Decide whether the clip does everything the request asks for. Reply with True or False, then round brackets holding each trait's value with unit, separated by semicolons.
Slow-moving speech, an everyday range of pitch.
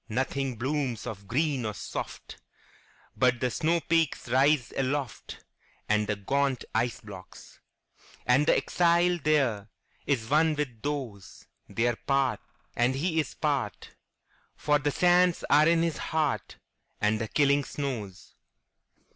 True (110 wpm; 4.7 semitones)